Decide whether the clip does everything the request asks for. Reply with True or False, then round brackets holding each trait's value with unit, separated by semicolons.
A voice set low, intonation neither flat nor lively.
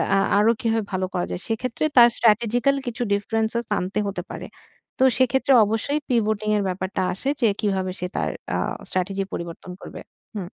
False (215 Hz; 3.8 semitones)